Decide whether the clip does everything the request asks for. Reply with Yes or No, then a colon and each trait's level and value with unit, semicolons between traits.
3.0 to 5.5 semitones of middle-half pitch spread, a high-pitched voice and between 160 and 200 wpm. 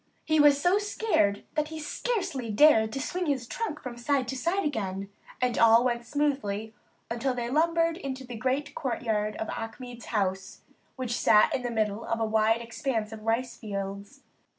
Yes: average, 4.9 semitones; high, 245 Hz; average, 175 wpm